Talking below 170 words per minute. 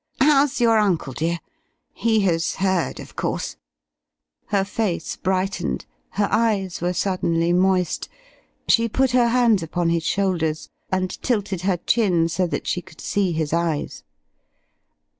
Yes: average, 140 wpm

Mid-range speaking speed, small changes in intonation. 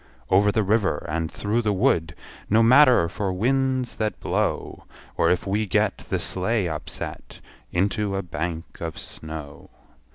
No: average, 150 wpm; average, 4.7 semitones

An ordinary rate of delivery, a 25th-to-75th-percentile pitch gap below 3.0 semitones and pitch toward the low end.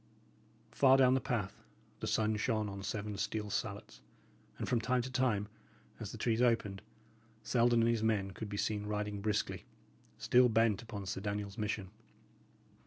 Yes: average, 165 wpm; narrow, 2.4 semitones; low, 110 Hz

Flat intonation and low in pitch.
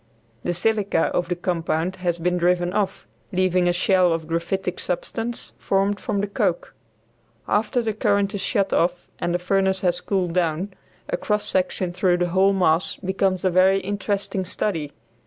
No: narrow, 2.0 semitones; medium, 185 Hz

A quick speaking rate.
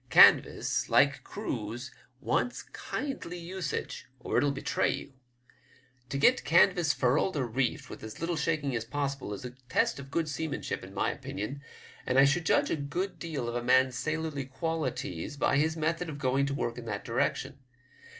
No: average, 175 wpm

